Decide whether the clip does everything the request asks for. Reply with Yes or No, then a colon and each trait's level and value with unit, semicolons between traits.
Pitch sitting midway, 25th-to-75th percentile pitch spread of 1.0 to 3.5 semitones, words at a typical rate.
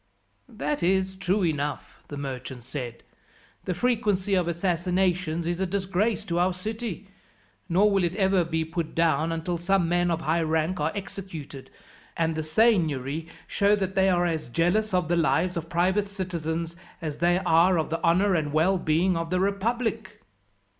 Yes: medium, 175 Hz; average, 2.9 semitones; average, 170 wpm